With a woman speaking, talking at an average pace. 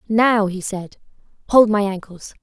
Yes: female; average, 150 wpm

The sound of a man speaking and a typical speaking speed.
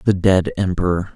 Yes: male; average, 155 wpm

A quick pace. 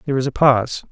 Yes: fast, 265 wpm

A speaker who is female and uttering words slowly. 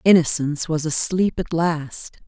Yes: female; slow, 130 wpm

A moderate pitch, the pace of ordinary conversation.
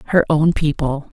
Yes: medium, 150 Hz; average, 150 wpm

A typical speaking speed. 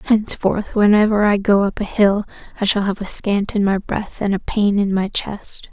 No: fast, 220 wpm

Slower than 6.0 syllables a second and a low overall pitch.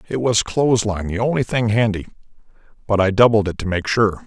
Yes: 5.7 syllables/s; low, 105 Hz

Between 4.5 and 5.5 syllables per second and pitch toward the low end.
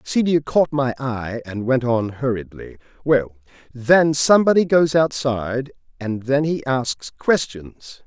No: 4.0 syllables/s; low, 130 Hz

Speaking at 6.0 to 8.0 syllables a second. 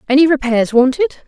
Yes: 6.5 syllables/s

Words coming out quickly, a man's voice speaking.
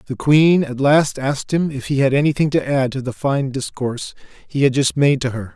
Yes: fast, 240 wpm; male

